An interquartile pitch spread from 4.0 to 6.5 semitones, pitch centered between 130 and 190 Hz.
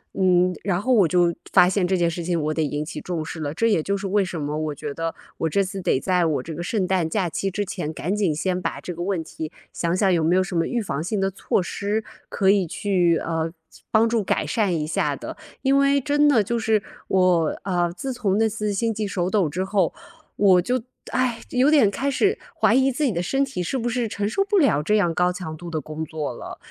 Yes: average, 4.5 semitones; medium, 185 Hz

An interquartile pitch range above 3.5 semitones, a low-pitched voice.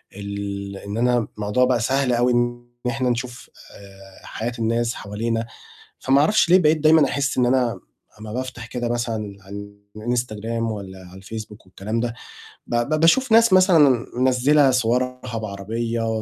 No: average, 3.2 semitones; low, 120 Hz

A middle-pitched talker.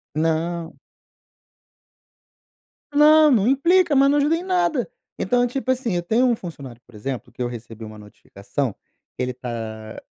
Yes: medium, 175 Hz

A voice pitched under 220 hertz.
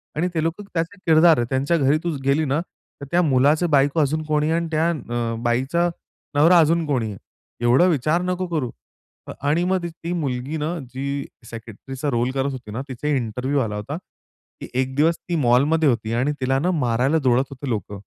Yes: medium, 140 Hz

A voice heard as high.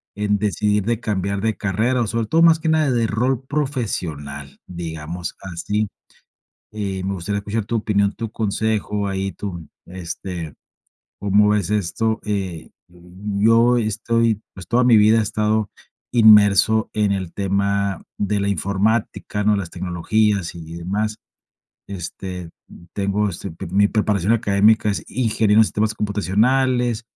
No: low, 105 Hz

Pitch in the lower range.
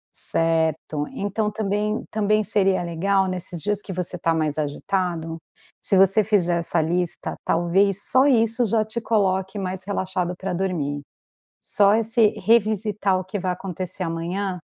No: high, 190 Hz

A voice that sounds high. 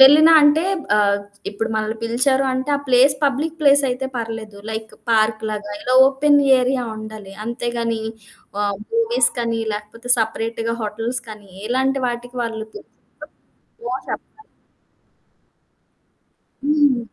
Yes: high, 235 Hz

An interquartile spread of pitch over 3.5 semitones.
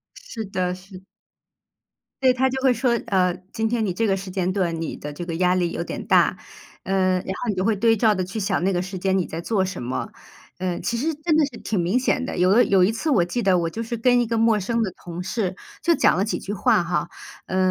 Yes: average, 4.0 semitones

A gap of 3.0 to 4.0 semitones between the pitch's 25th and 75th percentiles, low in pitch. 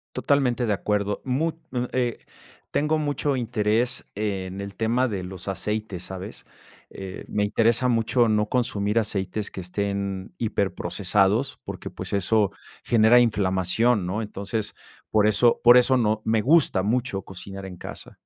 Yes: average, 3.5 semitones; low, 110 Hz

